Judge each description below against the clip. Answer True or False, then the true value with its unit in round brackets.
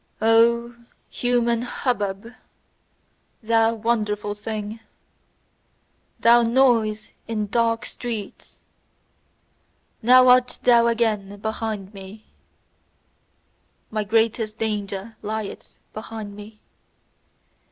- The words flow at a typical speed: False (80 wpm)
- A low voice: False (225 Hz)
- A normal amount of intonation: False (1.9 semitones)